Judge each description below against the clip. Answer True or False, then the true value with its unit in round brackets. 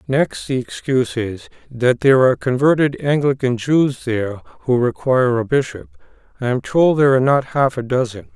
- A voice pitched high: False (130 Hz)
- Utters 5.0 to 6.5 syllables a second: True (5.2 syllables/s)